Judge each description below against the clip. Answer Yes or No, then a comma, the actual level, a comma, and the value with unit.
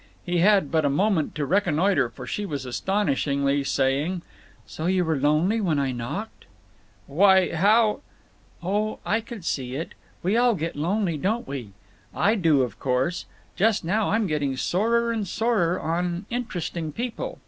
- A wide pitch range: Yes, wide, 6.3 semitones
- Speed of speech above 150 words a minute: Yes, average, 160 wpm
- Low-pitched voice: No, medium, 175 Hz